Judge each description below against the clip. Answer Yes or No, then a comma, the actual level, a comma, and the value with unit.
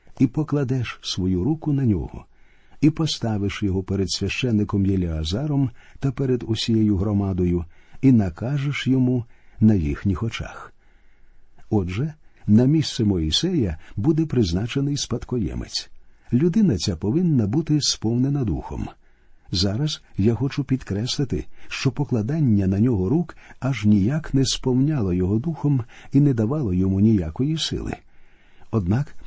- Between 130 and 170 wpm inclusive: No, average, 115 wpm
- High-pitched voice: No, low, 115 Hz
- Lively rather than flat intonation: Yes, wide, 5.7 semitones